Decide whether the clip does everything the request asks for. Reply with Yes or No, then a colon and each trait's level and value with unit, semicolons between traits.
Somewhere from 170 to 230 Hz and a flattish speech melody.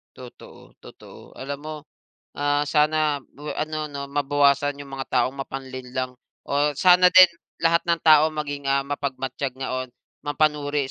No: medium, 145 Hz; narrow, 2.0 semitones